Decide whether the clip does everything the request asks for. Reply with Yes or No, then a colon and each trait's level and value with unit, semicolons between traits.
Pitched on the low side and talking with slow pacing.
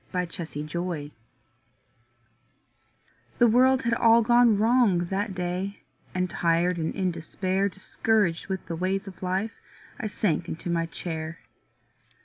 No: medium, 185 Hz; slow, 125 wpm